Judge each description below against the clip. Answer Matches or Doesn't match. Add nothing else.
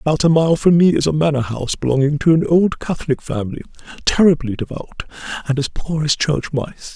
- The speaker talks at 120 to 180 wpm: Doesn't match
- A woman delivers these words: Doesn't match